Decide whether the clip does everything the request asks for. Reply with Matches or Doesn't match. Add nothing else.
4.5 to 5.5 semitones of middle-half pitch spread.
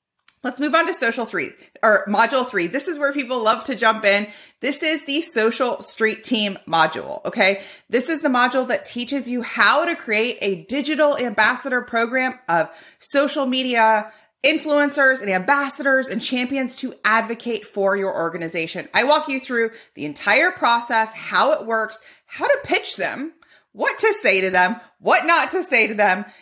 Matches